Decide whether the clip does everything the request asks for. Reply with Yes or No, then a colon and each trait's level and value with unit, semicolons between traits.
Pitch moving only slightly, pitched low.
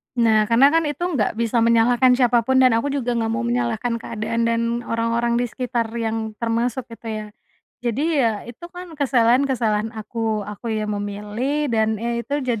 No: narrow, 2.1 semitones; high, 235 Hz